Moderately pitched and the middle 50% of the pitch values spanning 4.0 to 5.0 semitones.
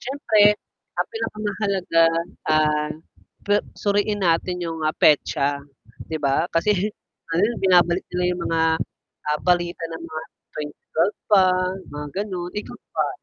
Yes: medium, 175 Hz; average, 4.4 semitones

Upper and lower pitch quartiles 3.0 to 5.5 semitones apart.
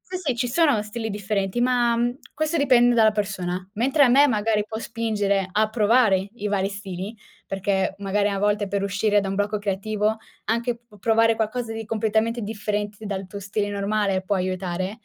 No: narrow, 2.4 semitones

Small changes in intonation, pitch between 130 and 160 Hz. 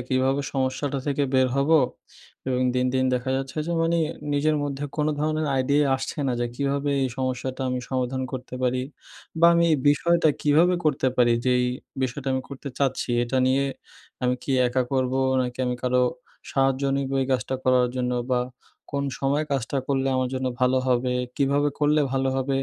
Yes: narrow, 1.9 semitones; low, 135 Hz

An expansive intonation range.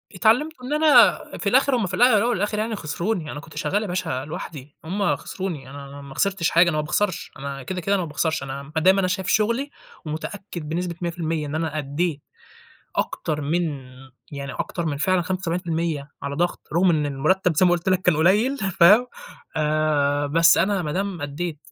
No: average, 4.0 semitones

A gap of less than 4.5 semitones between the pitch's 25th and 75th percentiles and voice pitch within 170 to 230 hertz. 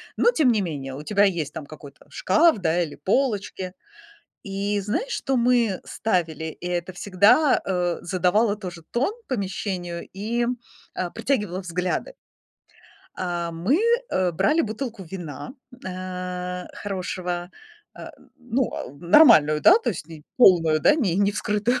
Yes: average, 4.0 semitones; medium, 185 Hz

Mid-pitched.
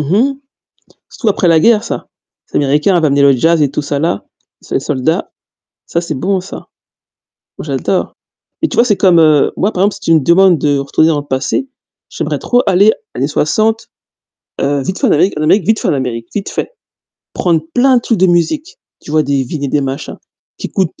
Yes: medium, 165 Hz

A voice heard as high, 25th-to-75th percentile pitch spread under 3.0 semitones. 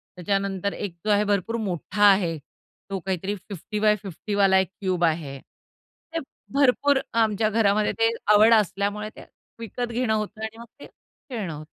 Yes: high, 205 Hz; narrow, 2.5 semitones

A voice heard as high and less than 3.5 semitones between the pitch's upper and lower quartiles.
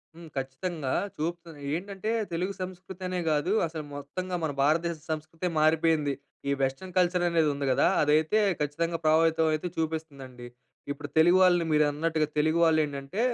No: medium, 160 Hz; average, 2.8 semitones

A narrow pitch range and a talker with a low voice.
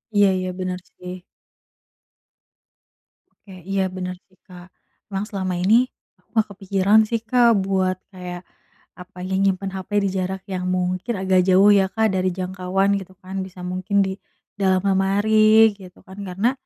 No: narrow, 1.5 semitones; high, 190 Hz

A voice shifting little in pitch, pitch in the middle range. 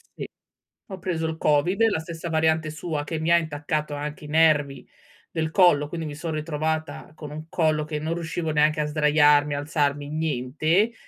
Yes: narrow, 1.5 semitones; medium, 155 Hz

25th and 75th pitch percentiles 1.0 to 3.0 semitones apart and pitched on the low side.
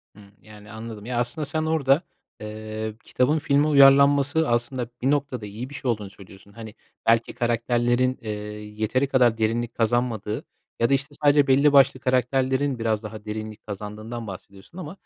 No: average, 4.1 semitones; low, 120 Hz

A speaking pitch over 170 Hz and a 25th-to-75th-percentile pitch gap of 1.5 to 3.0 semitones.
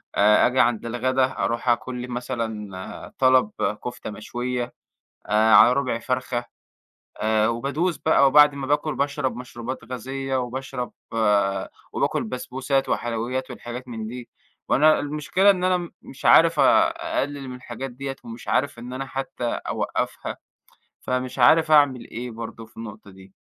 No: low, 125 Hz; average, 2.7 semitones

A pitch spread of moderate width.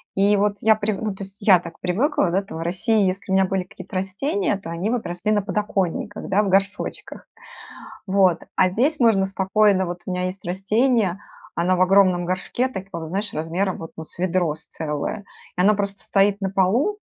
No: narrow, 2.3 semitones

